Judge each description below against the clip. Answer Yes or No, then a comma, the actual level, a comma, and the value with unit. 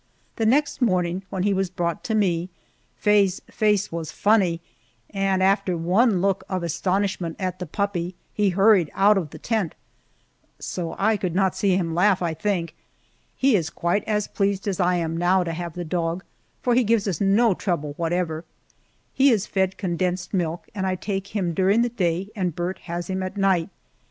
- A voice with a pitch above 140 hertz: Yes, high, 190 Hz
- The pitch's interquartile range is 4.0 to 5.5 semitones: No, average, 2.7 semitones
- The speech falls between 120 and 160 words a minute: No, average, 190 wpm